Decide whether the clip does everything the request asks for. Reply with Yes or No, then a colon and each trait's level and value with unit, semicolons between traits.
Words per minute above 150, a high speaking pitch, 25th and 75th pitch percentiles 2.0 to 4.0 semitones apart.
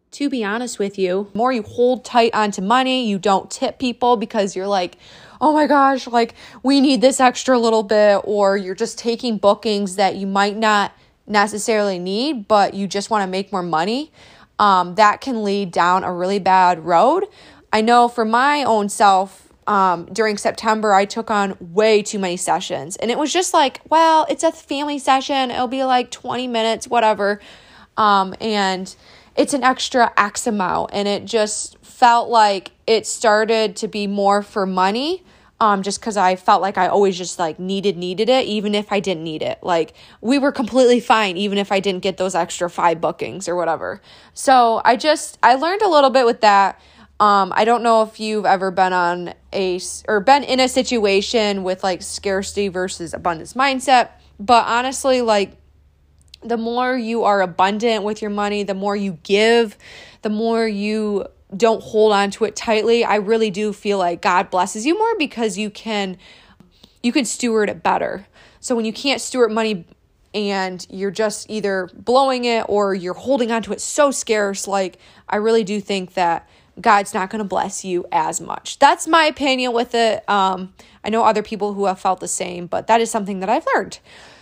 Yes: average, 200 wpm; high, 215 Hz; average, 3.4 semitones